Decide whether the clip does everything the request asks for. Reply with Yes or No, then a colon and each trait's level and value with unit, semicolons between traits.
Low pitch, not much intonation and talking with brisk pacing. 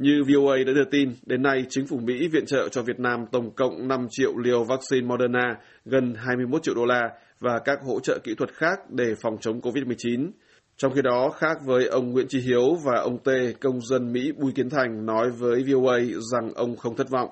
No: low, 125 Hz; narrow, 1.7 semitones; average, 220 wpm